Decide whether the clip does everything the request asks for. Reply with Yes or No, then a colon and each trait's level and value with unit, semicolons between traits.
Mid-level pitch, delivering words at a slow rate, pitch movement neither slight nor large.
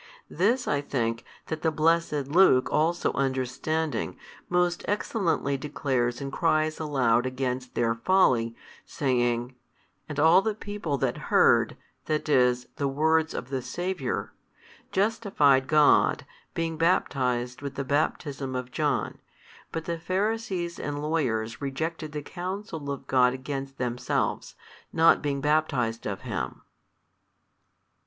Yes: medium, 145 Hz; slow, 125 wpm; average, 4.4 semitones